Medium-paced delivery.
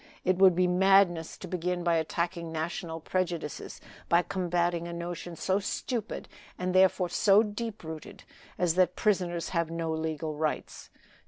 Yes: average, 150 wpm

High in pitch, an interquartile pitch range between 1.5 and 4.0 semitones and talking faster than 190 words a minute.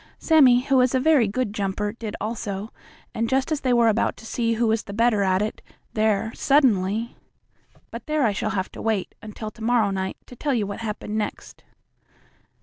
Yes: high, 225 Hz; average, 2.9 semitones; average, 200 wpm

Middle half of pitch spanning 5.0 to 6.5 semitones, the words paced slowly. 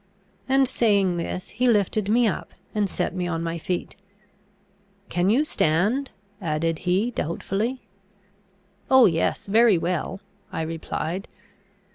Yes: average, 5.3 semitones; slow, 125 wpm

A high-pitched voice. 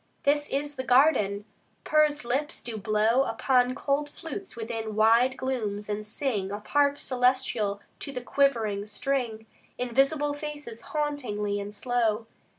Yes: very high, 250 Hz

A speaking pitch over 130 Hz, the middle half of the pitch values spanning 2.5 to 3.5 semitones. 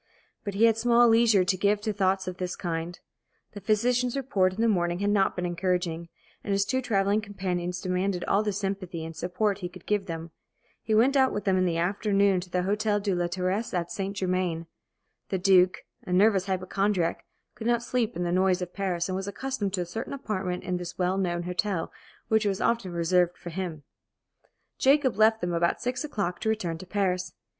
Yes: high, 190 Hz; average, 2.8 semitones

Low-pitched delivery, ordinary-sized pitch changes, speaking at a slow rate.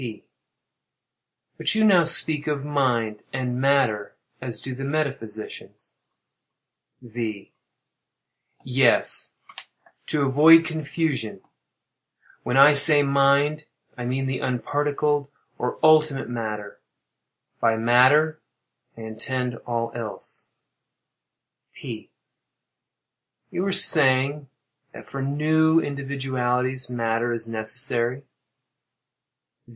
Yes: low, 130 Hz; average, 3.6 semitones; slow, 90 wpm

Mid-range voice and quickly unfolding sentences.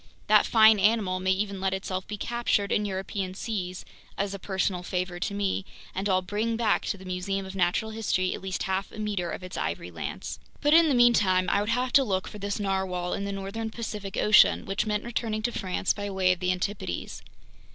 No: high, 195 Hz; fast, 210 wpm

